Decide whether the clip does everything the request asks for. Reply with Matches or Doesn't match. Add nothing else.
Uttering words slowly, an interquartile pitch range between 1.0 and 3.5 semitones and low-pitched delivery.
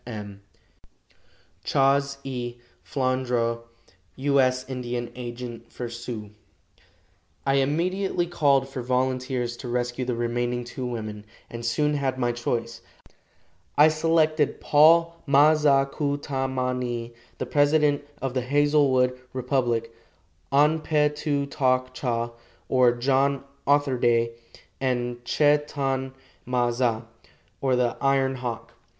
Matches